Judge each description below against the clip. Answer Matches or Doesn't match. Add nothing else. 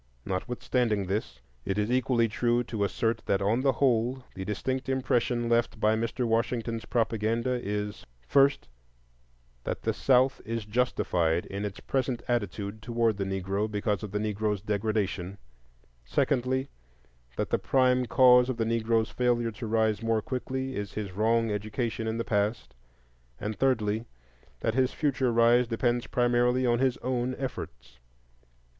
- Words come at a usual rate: Matches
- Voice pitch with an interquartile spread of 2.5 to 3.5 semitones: Matches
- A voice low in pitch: Matches